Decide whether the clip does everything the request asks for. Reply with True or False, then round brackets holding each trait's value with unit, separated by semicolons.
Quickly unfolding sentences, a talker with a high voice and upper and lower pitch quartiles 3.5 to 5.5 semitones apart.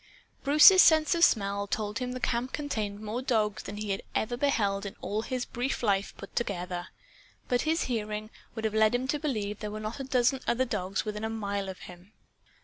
True (210 wpm; 220 Hz; 3.9 semitones)